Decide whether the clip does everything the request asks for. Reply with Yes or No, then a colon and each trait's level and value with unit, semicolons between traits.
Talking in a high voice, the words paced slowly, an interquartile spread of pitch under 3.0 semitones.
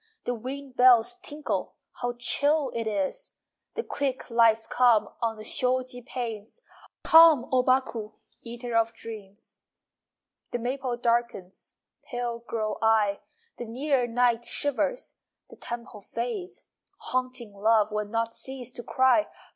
Yes: high, 240 Hz; slow, 130 wpm; narrow, 2.4 semitones